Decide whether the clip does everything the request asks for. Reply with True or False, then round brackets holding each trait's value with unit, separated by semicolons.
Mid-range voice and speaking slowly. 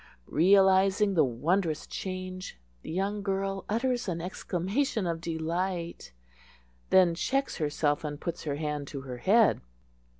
True (180 Hz; 130 wpm)